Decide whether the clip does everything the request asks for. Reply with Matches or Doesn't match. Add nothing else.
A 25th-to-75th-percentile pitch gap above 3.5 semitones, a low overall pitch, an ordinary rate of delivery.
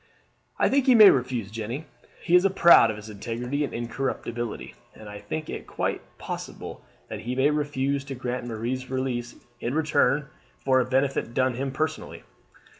Doesn't match